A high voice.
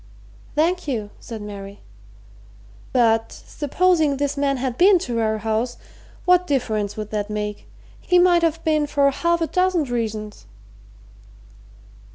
Yes: very high, 270 Hz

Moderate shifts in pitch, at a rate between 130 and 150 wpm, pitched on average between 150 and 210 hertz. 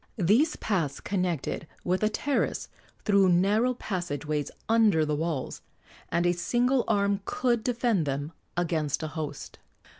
No: wide, 5.9 semitones; average, 140 wpm; medium, 185 Hz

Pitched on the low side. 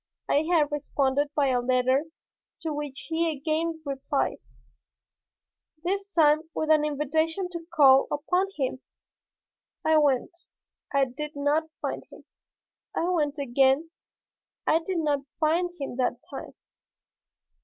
No: very high, 300 Hz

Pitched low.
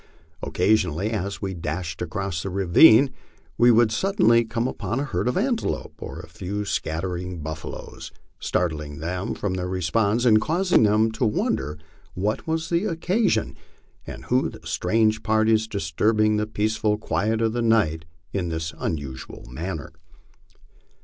Yes: low, 105 Hz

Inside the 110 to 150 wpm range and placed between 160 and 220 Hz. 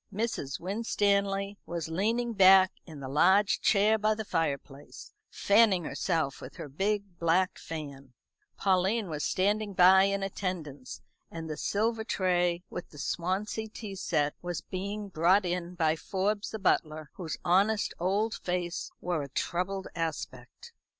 Yes: average, 145 wpm; medium, 185 Hz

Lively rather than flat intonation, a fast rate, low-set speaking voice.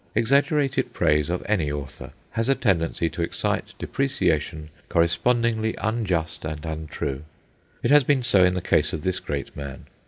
No: wide, 7.2 semitones; average, 155 wpm; very low, 90 Hz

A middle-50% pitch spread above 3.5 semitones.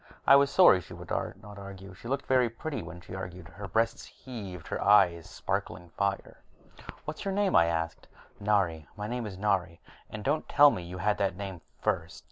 Yes: average, 4.5 semitones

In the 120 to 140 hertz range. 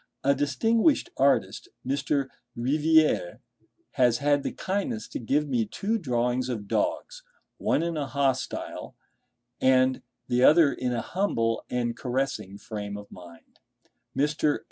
Yes: low, 135 Hz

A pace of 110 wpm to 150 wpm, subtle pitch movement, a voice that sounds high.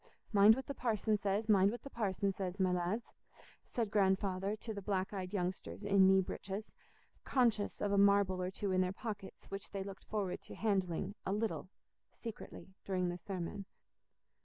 No: average, 180 wpm; narrow, 1.9 semitones; high, 200 Hz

